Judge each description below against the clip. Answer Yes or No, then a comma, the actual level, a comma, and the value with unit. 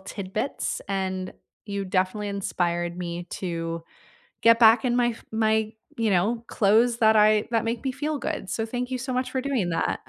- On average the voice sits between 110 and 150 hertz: No, high, 215 Hz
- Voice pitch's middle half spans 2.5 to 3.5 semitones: No, average, 4.2 semitones